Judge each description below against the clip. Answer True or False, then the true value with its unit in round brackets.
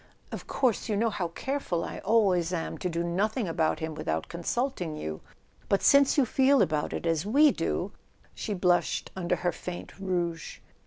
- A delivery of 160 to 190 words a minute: True (180 wpm)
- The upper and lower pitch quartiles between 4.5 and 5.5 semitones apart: True (5.2 semitones)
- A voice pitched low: False (180 Hz)